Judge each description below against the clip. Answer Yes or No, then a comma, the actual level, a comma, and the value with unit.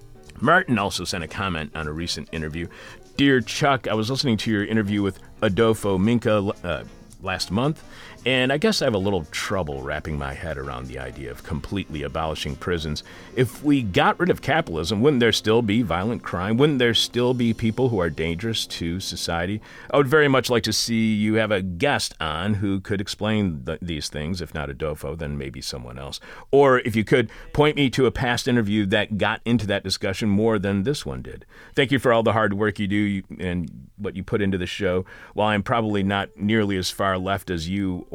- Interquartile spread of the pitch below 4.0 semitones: No, average, 5.1 semitones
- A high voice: No, low, 100 Hz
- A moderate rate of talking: No, fast, 210 wpm